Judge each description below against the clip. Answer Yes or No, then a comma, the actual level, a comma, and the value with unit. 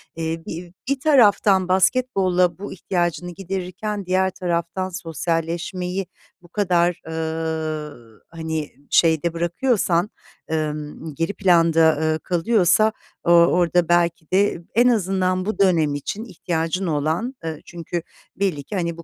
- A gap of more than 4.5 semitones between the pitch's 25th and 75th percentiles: No, narrow, 2.6 semitones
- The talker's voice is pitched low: No, medium, 175 Hz